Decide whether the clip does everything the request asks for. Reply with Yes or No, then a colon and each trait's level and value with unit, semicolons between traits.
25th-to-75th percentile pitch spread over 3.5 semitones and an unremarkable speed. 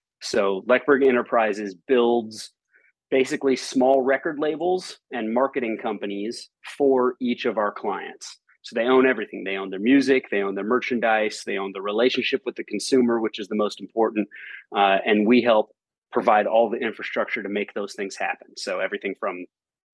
Yes: average, 4.0 semitones; average, 170 wpm